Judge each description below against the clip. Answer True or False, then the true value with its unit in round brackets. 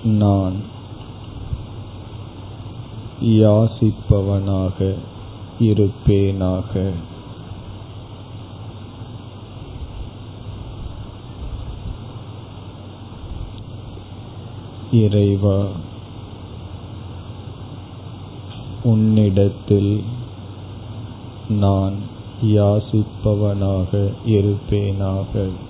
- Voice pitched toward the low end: True (105 Hz)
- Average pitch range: False (1.7 semitones)